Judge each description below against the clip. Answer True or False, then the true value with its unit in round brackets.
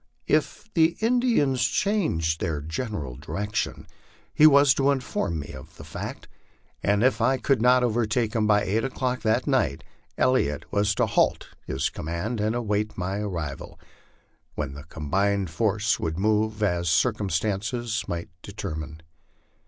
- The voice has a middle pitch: False (105 Hz)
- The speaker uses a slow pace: False (145 wpm)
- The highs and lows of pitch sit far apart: True (6.8 semitones)